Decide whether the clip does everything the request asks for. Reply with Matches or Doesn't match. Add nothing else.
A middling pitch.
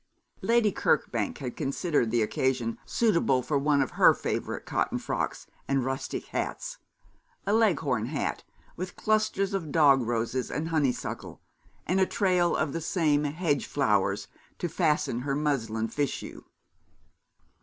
Matches